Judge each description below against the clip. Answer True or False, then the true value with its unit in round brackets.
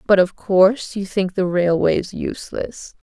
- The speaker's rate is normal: True (155 wpm)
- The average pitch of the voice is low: False (190 Hz)